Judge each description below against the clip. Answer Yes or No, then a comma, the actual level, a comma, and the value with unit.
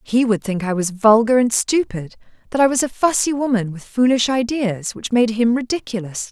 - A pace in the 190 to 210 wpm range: Yes, average, 200 wpm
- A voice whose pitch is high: Yes, high, 230 Hz